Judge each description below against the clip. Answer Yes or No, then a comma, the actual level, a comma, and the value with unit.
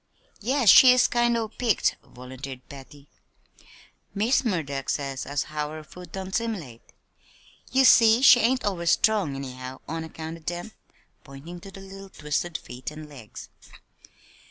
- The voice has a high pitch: No, medium, 170 Hz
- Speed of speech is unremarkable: Yes, average, 150 wpm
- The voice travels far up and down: Yes, wide, 7.8 semitones